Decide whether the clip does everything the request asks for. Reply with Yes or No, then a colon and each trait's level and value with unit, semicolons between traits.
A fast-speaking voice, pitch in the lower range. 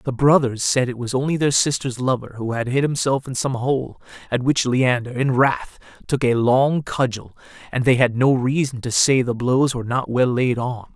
Yes: fast, 215 wpm; low, 125 Hz